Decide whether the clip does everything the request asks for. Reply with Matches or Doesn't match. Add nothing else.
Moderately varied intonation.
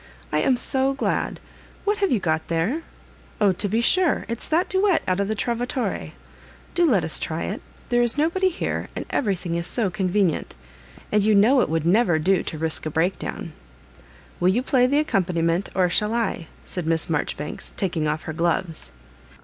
Doesn't match